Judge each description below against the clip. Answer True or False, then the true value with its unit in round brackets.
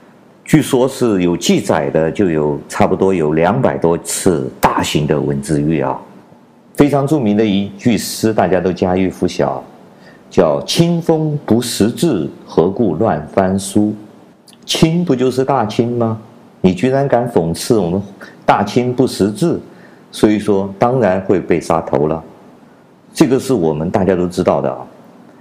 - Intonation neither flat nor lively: False (6.0 semitones)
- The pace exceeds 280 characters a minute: False (215 characters per minute)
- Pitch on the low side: True (105 Hz)